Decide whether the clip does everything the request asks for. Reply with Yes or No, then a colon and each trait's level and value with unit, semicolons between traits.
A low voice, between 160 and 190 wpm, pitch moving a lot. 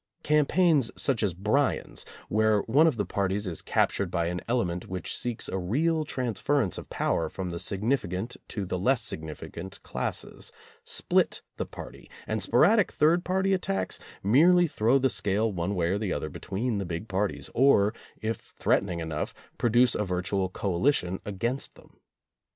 Yes: low, 105 Hz; average, 170 wpm; wide, 6.5 semitones